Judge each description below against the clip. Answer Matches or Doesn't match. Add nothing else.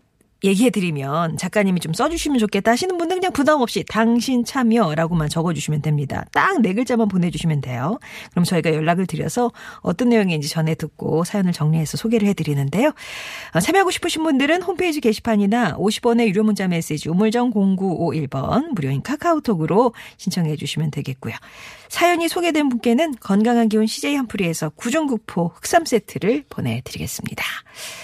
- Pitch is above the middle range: Matches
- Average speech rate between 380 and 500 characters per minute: Matches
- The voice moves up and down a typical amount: Doesn't match